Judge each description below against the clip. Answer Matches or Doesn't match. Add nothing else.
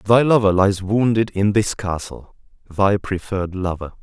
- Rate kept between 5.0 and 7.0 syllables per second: Doesn't match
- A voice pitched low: Matches